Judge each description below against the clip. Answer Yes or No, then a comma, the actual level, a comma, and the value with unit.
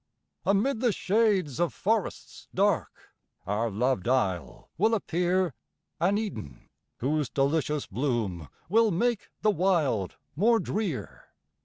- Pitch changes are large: Yes, wide, 8.2 semitones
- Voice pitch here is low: No, medium, 175 Hz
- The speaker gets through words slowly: Yes, slow, 115 wpm